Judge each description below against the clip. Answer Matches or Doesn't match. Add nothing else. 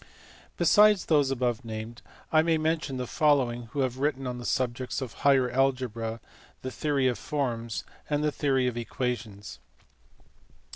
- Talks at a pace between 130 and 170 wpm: Matches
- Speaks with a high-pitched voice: Doesn't match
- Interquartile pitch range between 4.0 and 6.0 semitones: Doesn't match